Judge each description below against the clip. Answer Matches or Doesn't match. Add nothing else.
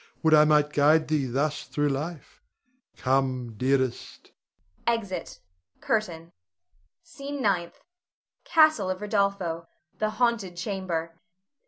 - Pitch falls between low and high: Matches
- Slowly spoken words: Matches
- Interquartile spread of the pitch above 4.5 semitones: Matches